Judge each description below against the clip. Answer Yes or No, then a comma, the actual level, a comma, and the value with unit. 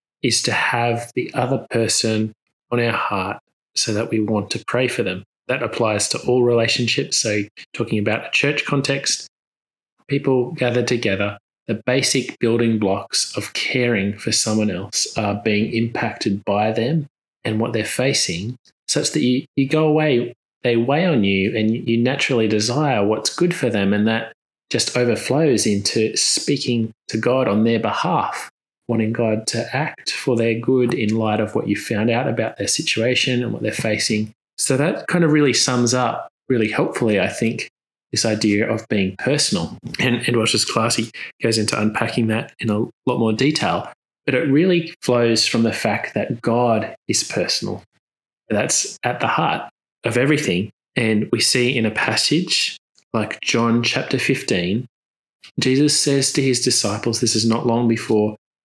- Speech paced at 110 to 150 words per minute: No, average, 170 wpm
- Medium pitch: No, low, 115 Hz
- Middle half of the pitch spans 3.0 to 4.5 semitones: No, narrow, 2.4 semitones